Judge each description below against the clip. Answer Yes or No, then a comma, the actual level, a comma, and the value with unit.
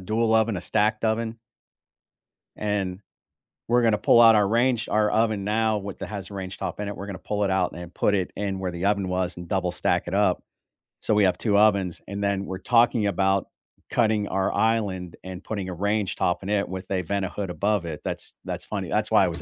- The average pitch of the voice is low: Yes, low, 100 Hz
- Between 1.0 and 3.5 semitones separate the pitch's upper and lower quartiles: Yes, narrow, 2.4 semitones